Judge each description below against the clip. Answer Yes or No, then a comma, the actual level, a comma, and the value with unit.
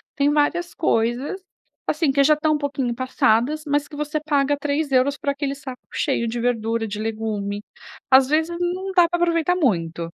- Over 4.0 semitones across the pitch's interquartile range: Yes, average, 4.5 semitones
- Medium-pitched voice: No, very high, 280 Hz